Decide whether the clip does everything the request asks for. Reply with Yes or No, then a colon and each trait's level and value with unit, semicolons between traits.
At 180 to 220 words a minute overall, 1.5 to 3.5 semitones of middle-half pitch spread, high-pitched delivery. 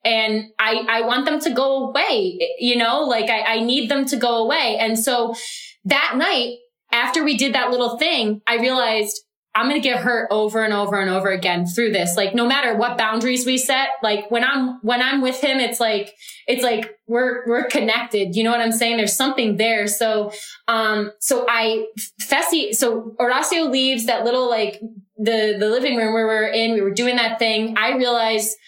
Yes: fast, 205 wpm; narrow, 2.6 semitones; high, 230 Hz